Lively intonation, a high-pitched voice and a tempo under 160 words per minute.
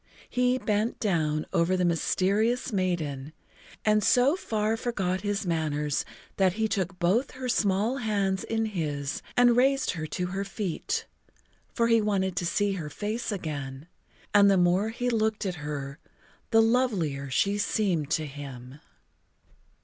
Yes: wide, 5.7 semitones; high, 195 Hz; average, 150 wpm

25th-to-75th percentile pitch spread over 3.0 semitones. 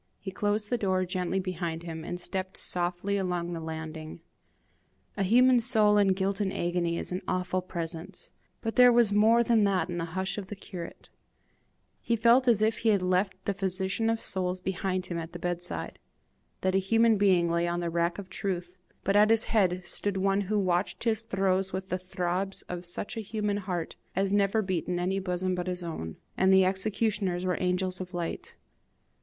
No: narrow, 2.5 semitones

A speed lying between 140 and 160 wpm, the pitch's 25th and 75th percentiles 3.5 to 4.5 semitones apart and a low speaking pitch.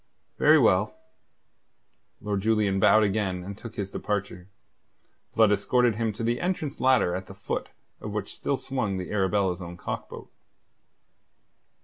No: average, 145 wpm; average, 2.8 semitones; low, 105 Hz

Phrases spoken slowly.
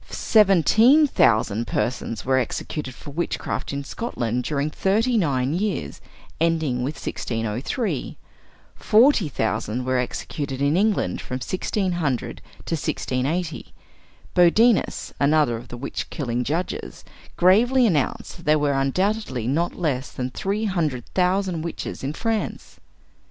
Yes: slow, 125 wpm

